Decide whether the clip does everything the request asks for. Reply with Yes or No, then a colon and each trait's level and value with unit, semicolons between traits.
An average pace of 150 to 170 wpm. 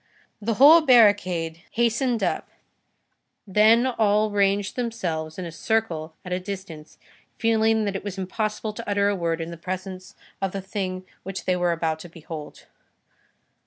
Yes: average, 160 wpm